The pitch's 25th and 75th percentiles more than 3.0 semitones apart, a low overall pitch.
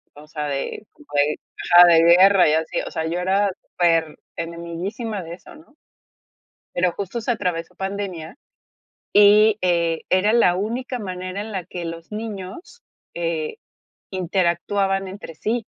No: average, 3.5 semitones; medium, 185 Hz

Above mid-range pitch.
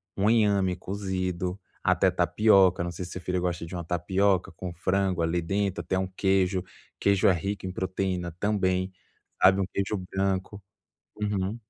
No: very low, 95 Hz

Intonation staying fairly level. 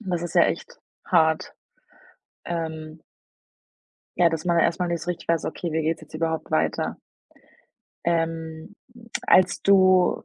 Yes: narrow, 1.7 semitones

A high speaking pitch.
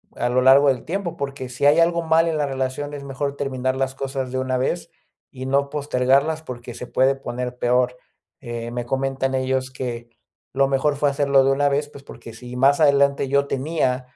No: low, 135 Hz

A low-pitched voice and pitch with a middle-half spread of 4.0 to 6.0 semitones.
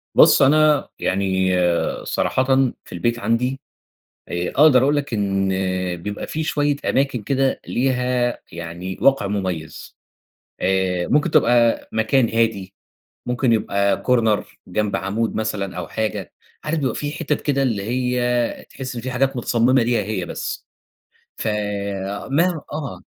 Yes: low, 120 Hz; average, 4.9 semitones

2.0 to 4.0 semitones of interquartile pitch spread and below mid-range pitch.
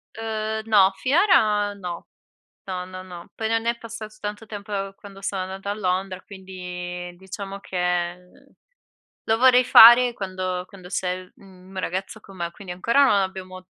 No: average, 2.7 semitones; high, 195 Hz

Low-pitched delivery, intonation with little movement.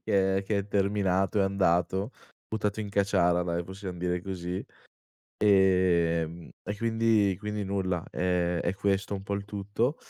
Yes: very low, 95 Hz; narrow, 2.2 semitones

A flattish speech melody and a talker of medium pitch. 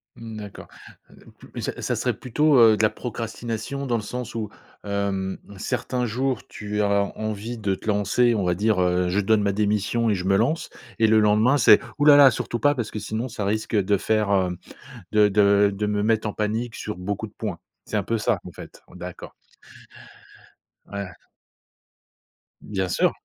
No: narrow, 2.3 semitones; low, 105 Hz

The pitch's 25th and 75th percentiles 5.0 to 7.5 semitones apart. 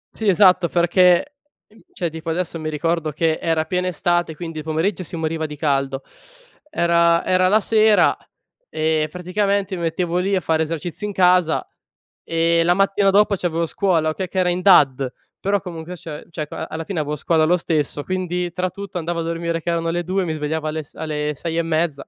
No: narrow, 2.5 semitones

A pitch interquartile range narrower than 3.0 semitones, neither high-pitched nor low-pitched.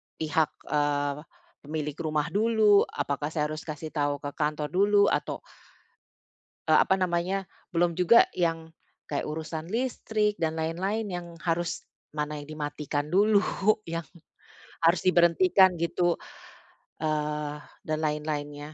No: average, 3.4 semitones; medium, 160 Hz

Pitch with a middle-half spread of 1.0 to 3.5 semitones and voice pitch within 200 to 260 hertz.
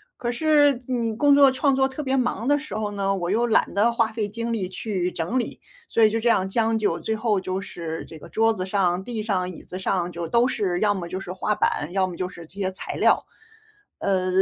No: average, 4.2 semitones; high, 210 Hz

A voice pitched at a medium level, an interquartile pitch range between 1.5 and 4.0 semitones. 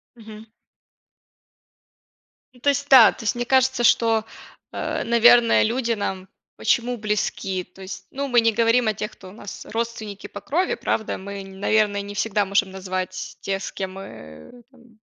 No: high, 215 Hz; average, 3.5 semitones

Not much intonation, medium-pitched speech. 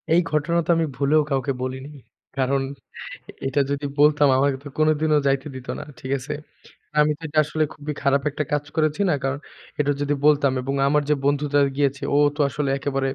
Yes: narrow, 1.6 semitones; medium, 145 Hz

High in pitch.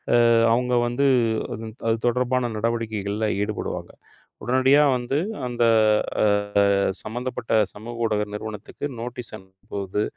No: low, 115 Hz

